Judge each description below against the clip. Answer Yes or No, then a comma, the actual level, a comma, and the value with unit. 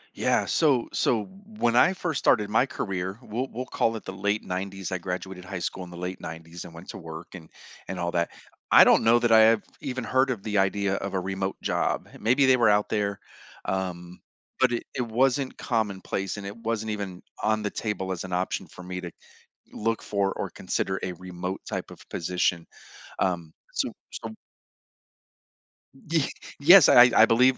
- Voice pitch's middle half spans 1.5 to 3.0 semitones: No, average, 4.0 semitones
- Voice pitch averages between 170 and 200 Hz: No, low, 100 Hz